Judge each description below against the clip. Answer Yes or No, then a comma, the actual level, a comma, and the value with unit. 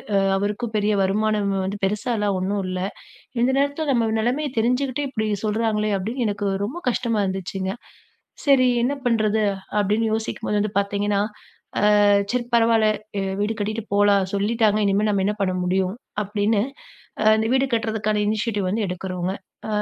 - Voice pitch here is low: No, high, 215 Hz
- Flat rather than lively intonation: Yes, narrow, 2.3 semitones